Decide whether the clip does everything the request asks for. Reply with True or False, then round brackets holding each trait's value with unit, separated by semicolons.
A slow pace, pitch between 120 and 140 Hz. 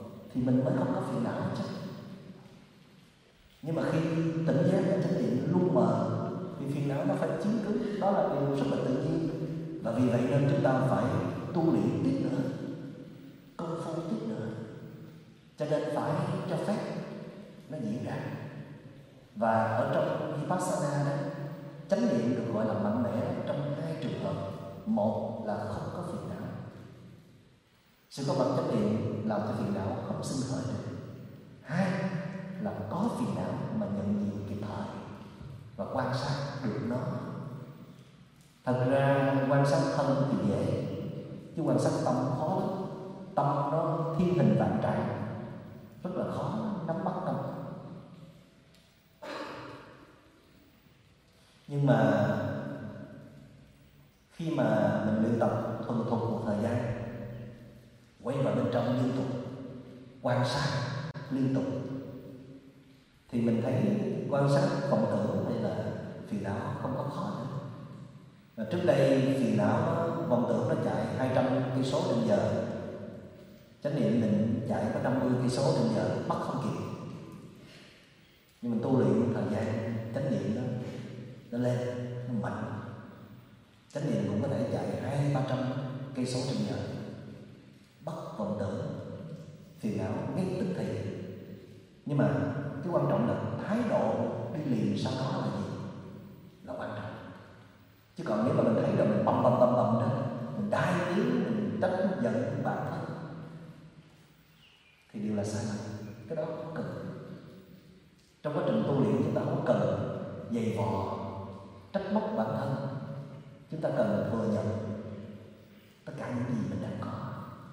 True (150 wpm; 135 Hz)